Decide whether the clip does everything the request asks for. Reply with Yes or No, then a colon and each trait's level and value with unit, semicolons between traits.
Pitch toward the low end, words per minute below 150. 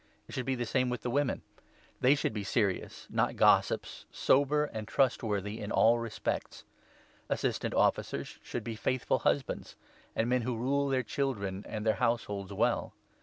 No: low, 120 Hz; average, 170 wpm